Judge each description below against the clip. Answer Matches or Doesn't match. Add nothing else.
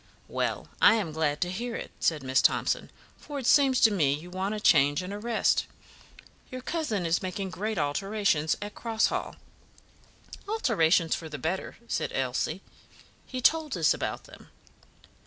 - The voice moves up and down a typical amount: Doesn't match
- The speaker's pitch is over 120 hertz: Matches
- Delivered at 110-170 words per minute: Matches